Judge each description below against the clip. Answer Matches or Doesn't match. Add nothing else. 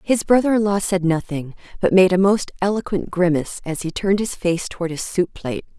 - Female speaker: Matches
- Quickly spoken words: Matches